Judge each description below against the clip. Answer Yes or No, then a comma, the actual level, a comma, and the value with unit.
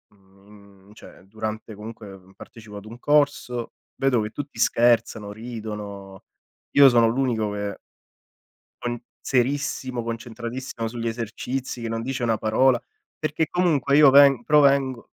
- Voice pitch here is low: Yes, low, 115 Hz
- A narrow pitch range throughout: No, average, 3.7 semitones